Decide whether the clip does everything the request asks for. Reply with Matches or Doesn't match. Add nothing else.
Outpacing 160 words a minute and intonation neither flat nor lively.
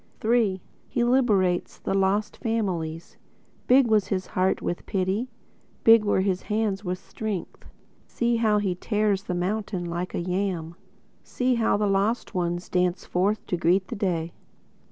Doesn't match